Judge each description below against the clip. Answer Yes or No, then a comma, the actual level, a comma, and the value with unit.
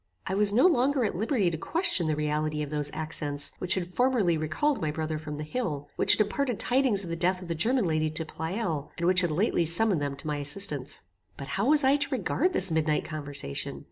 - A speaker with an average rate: No, fast, 230 wpm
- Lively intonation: Yes, wide, 6.6 semitones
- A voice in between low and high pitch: Yes, medium, 170 Hz